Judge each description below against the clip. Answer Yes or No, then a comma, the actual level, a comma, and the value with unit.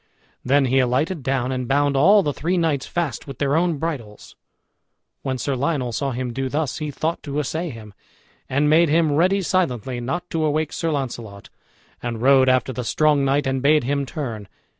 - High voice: No, medium, 140 Hz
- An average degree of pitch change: Yes, average, 3.4 semitones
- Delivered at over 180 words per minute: Yes, average, 190 wpm